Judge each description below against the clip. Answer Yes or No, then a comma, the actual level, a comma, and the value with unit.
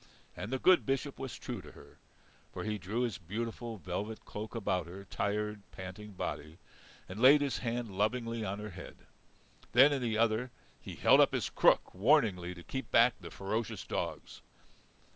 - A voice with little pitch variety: No, average, 3.7 semitones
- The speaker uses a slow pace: No, average, 175 wpm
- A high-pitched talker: No, low, 110 Hz